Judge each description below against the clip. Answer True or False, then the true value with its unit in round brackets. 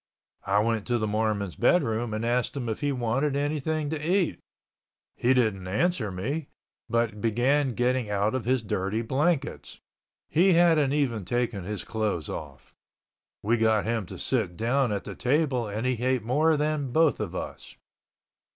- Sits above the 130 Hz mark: False (120 Hz)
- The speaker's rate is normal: True (165 wpm)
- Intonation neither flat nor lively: True (4.8 semitones)